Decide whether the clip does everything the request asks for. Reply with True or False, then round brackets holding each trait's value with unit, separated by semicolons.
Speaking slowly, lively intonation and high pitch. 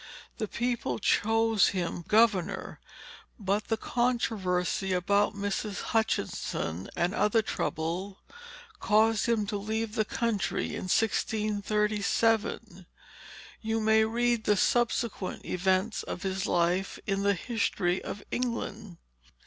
False (110 wpm; 2.8 semitones; 210 Hz)